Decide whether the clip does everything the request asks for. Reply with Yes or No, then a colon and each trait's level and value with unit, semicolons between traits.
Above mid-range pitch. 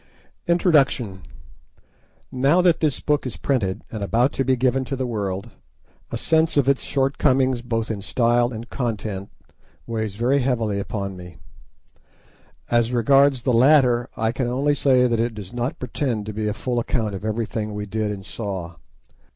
No: low, 120 Hz